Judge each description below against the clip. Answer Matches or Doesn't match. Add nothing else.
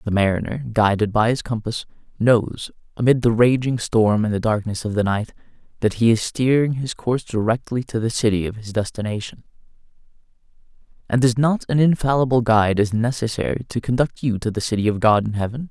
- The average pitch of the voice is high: Doesn't match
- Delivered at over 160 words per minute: Matches